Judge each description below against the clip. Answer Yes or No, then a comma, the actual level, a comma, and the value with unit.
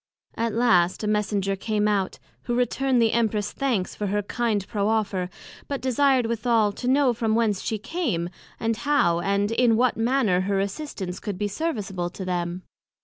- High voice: Yes, high, 215 Hz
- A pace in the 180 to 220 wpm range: No, average, 170 wpm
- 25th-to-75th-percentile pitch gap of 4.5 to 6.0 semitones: No, average, 3.6 semitones